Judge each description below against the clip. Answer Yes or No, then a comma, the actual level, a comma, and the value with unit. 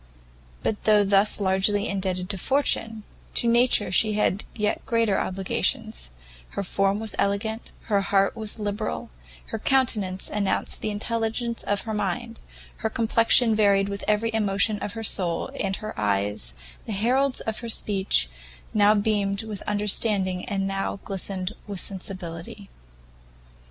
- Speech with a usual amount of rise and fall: No, narrow, 2.2 semitones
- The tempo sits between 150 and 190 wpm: No, average, 140 wpm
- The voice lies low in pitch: No, high, 205 Hz